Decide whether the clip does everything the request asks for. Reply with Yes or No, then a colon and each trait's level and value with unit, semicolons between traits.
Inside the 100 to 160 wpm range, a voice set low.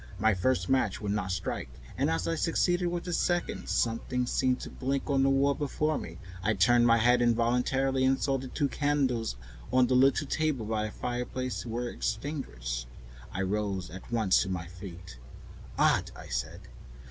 No: average, 180 wpm; low, 120 Hz